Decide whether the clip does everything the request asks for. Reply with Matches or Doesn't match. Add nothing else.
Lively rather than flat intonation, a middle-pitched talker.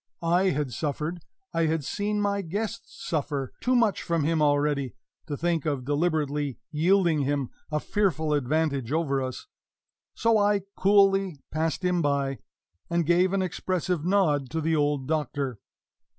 Doesn't match